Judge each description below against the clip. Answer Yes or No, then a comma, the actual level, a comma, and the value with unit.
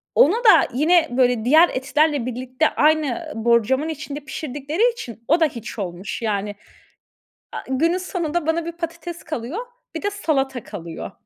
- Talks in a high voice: Yes, very high, 295 Hz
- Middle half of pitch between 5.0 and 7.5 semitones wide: Yes, average, 5.3 semitones